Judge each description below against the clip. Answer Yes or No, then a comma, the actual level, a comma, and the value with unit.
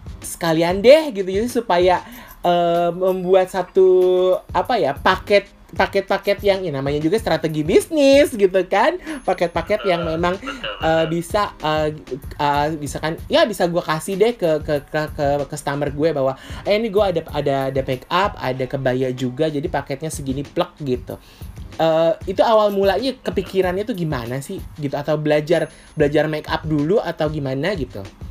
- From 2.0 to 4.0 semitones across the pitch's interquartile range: No, average, 5.0 semitones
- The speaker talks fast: Yes, fast, 155 wpm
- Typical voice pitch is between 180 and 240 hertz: No, medium, 165 Hz